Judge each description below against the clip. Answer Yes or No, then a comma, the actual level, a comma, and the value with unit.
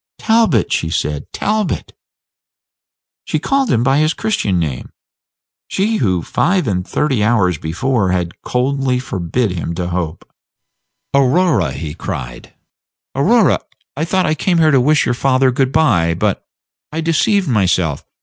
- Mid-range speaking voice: No, low, 125 Hz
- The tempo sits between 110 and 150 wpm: Yes, average, 140 wpm